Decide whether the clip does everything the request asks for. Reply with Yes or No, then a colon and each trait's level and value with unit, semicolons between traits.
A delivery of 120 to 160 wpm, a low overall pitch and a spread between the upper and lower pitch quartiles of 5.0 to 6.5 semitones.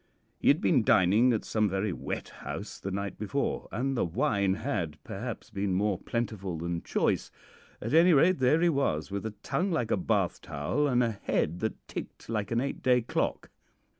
No: average, 195 wpm; low, 110 Hz; average, 5.3 semitones